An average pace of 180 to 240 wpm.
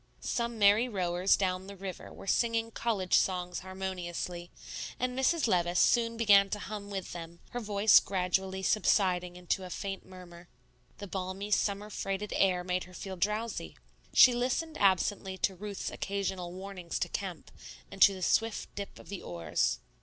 No: average, 160 wpm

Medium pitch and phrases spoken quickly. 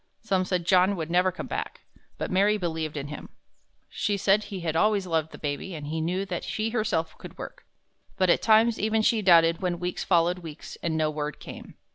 Yes: medium, 180 Hz; fast, 215 wpm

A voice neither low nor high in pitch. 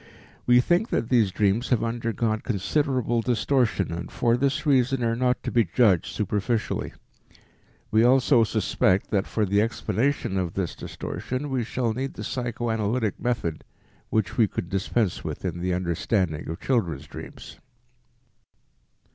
No: low, 115 Hz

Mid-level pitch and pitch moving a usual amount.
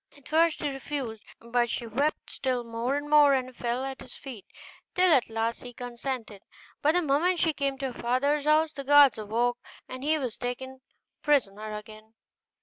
No: very high, 260 Hz; average, 3.6 semitones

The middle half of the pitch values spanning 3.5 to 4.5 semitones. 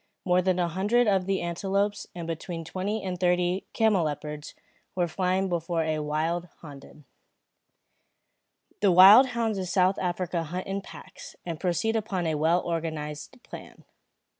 No: average, 2.8 semitones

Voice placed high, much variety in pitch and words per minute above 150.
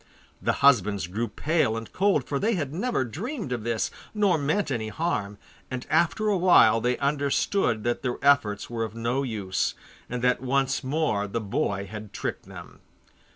No: low, 125 Hz; wide, 6.0 semitones; average, 175 wpm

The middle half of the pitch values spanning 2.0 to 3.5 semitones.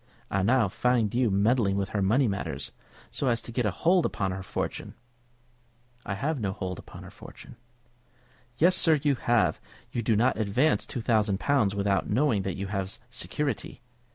No: average, 4.6 semitones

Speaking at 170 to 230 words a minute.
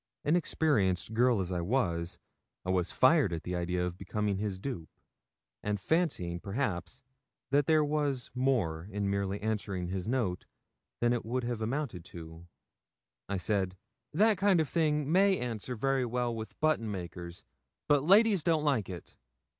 No: average, 155 wpm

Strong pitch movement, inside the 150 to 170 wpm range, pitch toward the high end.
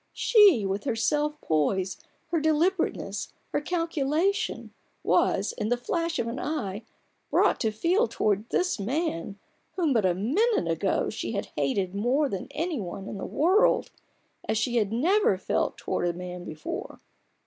Yes: wide, 9.0 semitones; average, 160 wpm; high, 240 Hz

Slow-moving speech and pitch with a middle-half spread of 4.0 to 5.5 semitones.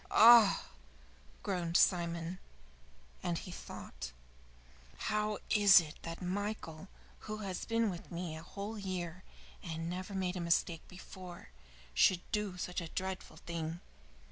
No: slow, 130 wpm; average, 2.8 semitones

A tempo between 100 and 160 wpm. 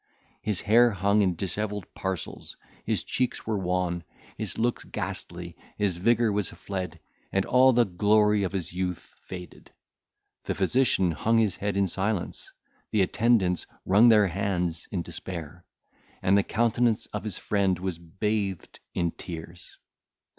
Yes: average, 145 wpm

